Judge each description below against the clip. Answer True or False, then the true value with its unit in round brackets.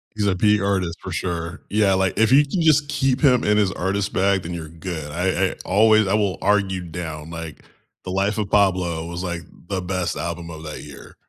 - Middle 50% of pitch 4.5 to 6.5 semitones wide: False (3.3 semitones)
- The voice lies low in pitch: True (95 Hz)